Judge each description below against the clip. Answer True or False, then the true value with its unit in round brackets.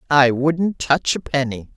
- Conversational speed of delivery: True (170 wpm)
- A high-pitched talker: False (140 Hz)